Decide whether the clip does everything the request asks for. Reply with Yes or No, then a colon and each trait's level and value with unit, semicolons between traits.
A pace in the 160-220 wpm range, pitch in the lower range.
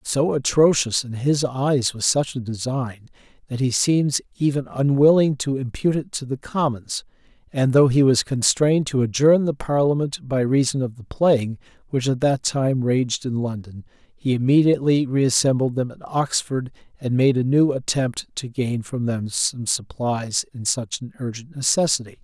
Yes: average, 170 wpm; low, 130 Hz